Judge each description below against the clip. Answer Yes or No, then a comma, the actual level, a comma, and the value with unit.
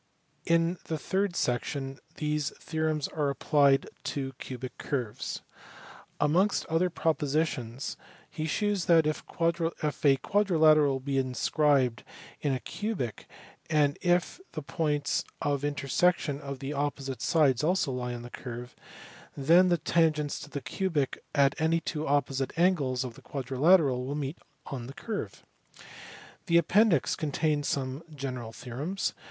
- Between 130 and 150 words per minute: Yes, slow, 135 wpm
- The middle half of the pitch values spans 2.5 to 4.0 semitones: Yes, average, 3.6 semitones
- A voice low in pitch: No, medium, 145 Hz